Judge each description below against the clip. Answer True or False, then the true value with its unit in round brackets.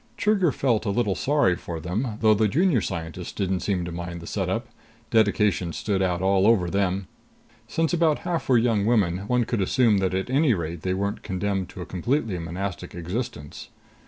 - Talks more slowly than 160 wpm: False (190 wpm)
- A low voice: True (100 Hz)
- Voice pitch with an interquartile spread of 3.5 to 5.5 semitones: True (4.8 semitones)